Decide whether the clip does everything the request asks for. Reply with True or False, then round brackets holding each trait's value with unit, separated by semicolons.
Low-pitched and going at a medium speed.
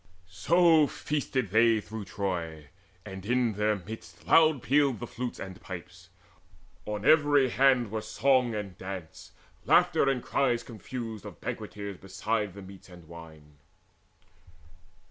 False (110 Hz; 130 wpm)